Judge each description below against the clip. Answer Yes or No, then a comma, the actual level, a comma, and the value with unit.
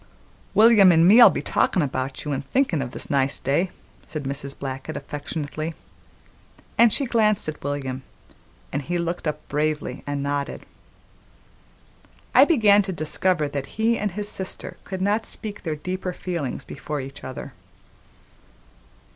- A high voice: No, medium, 155 Hz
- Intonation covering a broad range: Yes, wide, 5.7 semitones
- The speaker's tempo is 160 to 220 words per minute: No, average, 145 wpm